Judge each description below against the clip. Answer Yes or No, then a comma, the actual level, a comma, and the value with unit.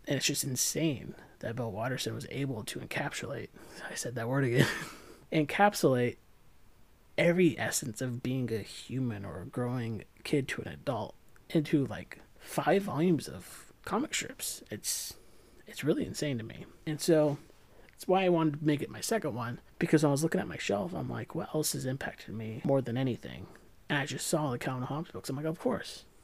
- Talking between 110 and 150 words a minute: No, average, 195 wpm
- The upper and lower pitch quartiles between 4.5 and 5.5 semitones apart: Yes, average, 4.8 semitones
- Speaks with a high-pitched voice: No, low, 135 Hz